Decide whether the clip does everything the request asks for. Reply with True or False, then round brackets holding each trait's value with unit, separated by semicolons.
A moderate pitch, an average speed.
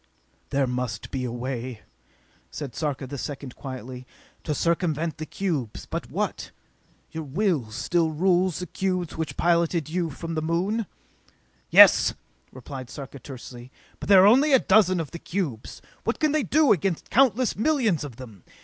True (160 Hz; 160 wpm)